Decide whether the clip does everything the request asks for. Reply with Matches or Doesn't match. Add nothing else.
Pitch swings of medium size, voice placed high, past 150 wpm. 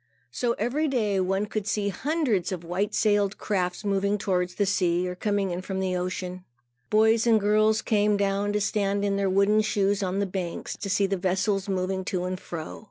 Doesn't match